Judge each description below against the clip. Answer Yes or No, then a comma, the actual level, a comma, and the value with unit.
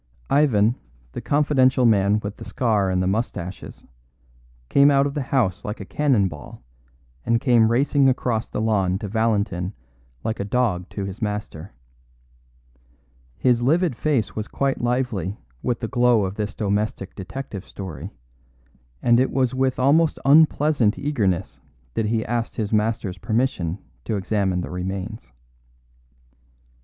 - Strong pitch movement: No, average, 4.6 semitones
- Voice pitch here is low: Yes, low, 110 Hz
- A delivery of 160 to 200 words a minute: No, average, 145 wpm